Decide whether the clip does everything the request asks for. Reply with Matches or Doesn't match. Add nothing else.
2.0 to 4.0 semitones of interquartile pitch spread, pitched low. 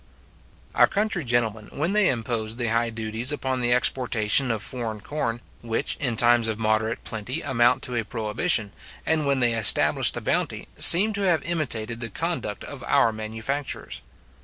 Matches